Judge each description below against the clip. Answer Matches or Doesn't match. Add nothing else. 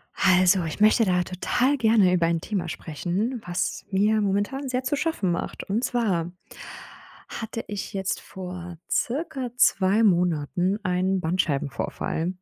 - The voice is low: Doesn't match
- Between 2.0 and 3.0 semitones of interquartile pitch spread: Doesn't match